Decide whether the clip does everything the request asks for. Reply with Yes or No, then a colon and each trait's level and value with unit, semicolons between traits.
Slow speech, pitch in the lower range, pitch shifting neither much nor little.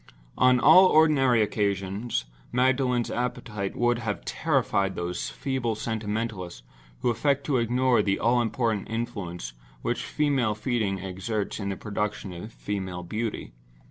Yes: slow, 130 wpm; low, 110 Hz; average, 3.8 semitones